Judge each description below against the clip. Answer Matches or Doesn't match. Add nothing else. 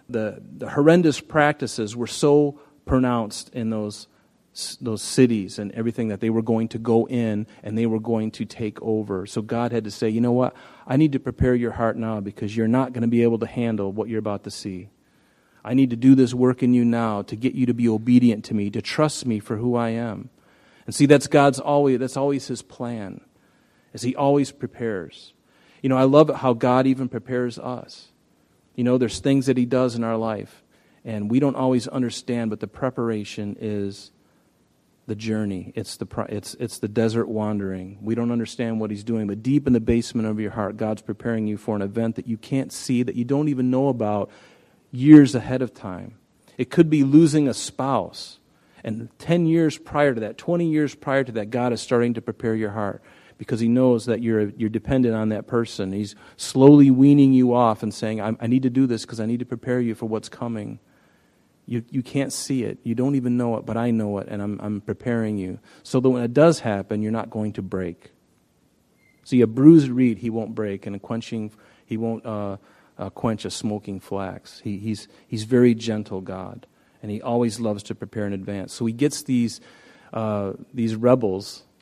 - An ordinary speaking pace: Doesn't match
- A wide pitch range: Doesn't match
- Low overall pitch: Matches